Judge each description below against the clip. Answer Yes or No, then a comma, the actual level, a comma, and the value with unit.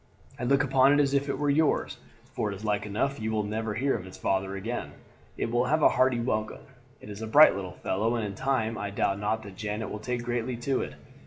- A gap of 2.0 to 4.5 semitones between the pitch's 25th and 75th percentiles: Yes, average, 4.1 semitones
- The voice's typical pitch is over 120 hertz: No, low, 115 Hz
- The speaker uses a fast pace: Yes, fast, 250 wpm